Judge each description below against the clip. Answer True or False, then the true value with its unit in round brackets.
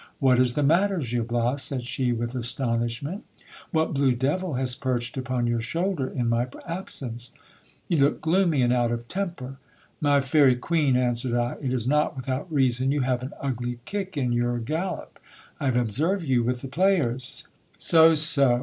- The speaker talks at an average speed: True (180 wpm)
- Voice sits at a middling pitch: False (130 Hz)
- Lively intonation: False (4.0 semitones)